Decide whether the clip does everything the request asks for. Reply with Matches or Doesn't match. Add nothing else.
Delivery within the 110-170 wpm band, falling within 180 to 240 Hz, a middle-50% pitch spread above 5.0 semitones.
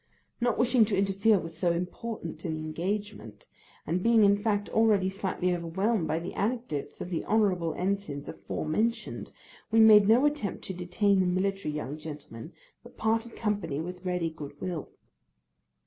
Doesn't match